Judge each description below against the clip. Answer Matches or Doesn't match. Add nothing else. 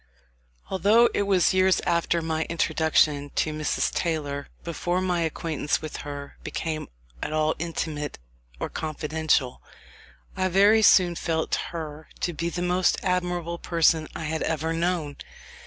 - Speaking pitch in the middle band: Matches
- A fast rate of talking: Doesn't match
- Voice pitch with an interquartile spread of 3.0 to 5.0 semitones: Doesn't match